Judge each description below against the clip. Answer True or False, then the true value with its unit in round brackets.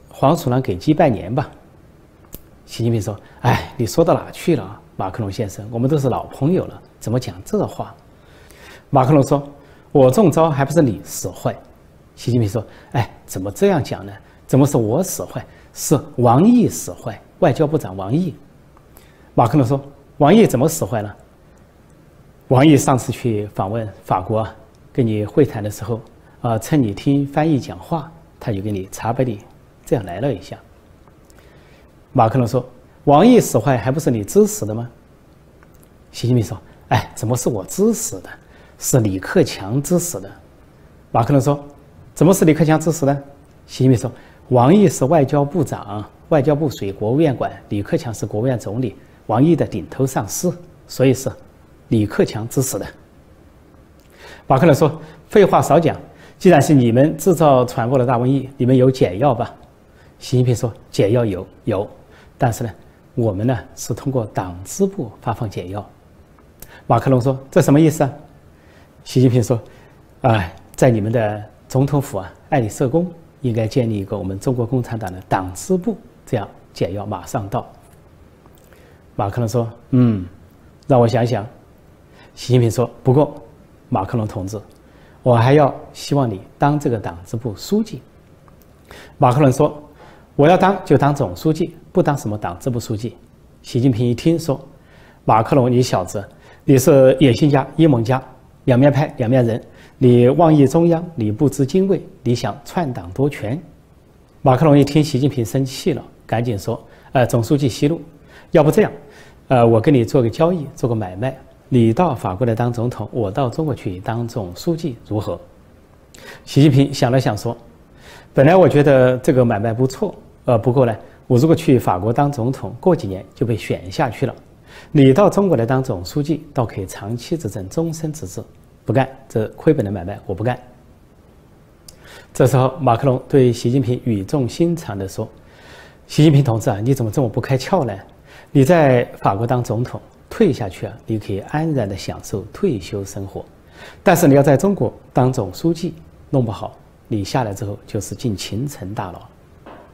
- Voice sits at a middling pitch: False (125 Hz)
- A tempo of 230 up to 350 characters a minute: True (250 characters per minute)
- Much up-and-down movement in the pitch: False (4.9 semitones)